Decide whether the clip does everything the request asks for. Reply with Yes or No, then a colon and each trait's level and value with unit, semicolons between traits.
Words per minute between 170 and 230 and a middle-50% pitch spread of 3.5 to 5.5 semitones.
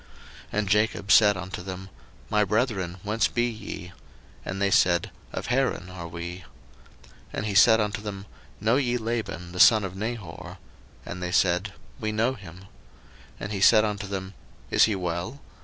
No: average, 175 wpm; average, 3.1 semitones